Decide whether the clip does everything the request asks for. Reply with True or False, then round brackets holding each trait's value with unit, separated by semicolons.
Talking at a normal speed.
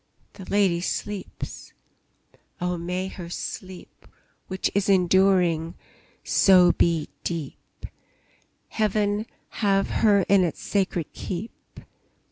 False (95 wpm)